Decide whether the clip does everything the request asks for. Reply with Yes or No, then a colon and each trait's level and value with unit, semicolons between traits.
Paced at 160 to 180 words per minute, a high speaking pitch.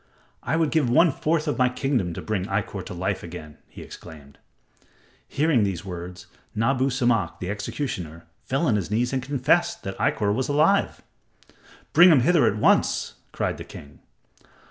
No: average, 165 wpm; low, 120 Hz